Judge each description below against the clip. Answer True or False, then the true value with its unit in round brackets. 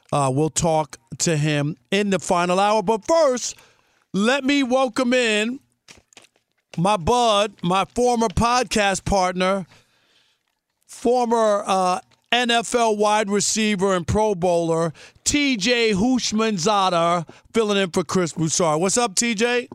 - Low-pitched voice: False (205 Hz)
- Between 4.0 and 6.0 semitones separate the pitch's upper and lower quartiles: True (4.6 semitones)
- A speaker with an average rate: False (120 wpm)